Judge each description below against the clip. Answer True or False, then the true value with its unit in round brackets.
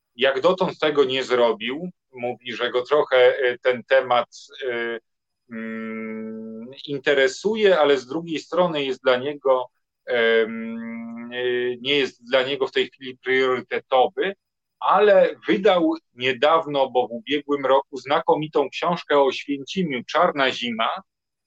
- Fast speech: False (115 wpm)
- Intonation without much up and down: False (3.6 semitones)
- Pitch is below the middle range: True (130 Hz)